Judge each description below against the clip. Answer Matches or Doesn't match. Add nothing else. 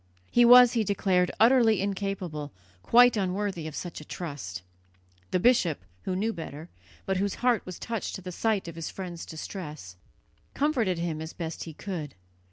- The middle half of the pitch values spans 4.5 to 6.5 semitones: Matches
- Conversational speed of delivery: Matches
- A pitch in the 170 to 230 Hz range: Matches